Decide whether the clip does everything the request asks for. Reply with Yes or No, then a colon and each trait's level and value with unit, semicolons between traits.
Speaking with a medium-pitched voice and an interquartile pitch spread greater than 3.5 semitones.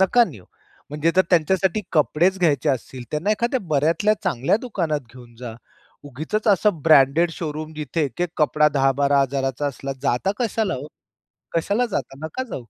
Yes: medium, 155 Hz; wide, 5.6 semitones